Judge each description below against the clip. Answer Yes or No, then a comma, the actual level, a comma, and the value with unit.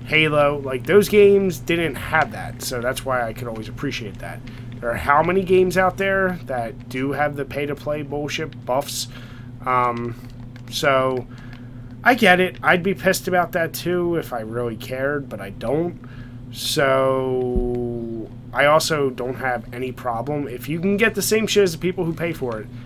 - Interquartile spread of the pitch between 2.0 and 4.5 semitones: No, average, 5.1 semitones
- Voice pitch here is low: Yes, low, 130 Hz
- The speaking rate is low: No, average, 185 wpm